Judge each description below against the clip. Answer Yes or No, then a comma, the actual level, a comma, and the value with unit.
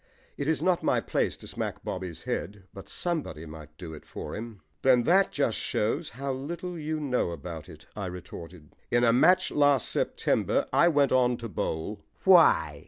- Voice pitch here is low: Yes, low, 120 Hz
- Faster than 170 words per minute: Yes, average, 185 wpm